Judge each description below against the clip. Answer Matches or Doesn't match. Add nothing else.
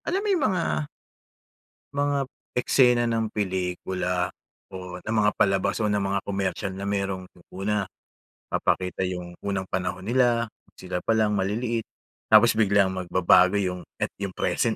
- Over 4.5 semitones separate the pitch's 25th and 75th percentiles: Doesn't match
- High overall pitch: Doesn't match